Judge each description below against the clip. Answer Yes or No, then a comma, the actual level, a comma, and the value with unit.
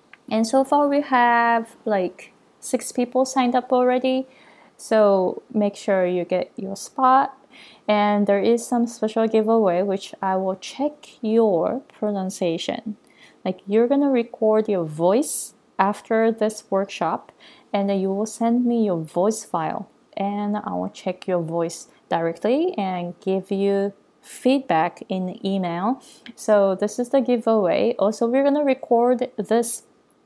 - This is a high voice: Yes, high, 215 Hz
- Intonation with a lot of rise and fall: No, average, 4.1 semitones